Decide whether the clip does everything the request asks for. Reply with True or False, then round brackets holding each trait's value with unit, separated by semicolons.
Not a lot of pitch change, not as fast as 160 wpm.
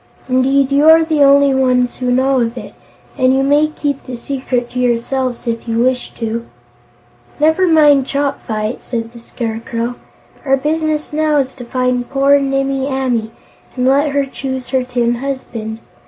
False (2.3 semitones; 165 wpm)